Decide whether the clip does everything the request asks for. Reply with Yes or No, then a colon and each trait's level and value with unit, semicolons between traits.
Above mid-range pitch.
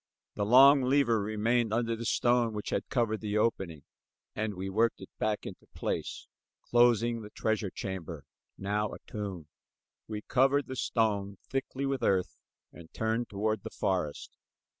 No: low, 110 Hz